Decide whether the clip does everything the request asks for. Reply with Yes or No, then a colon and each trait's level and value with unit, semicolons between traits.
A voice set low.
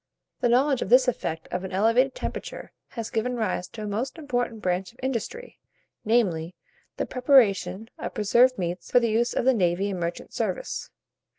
No: high, 225 Hz